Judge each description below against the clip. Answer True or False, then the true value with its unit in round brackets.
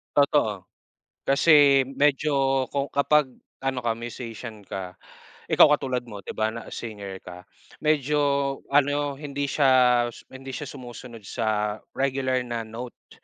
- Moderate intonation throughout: True (3.6 semitones)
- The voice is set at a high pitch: False (130 Hz)